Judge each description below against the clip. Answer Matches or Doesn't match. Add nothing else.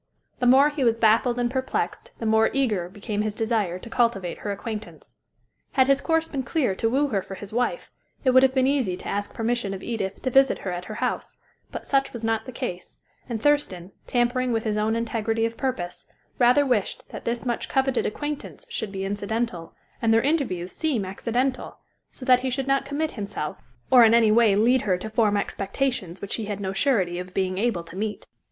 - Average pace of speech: Doesn't match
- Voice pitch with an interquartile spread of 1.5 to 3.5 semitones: Doesn't match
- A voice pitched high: Matches